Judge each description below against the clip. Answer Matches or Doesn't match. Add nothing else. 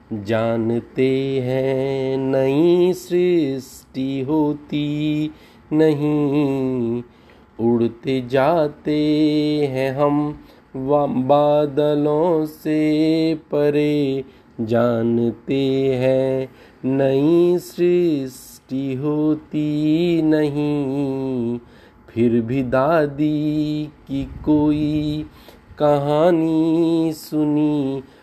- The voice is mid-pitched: Matches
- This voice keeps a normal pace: Doesn't match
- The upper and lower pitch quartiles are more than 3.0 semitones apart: Doesn't match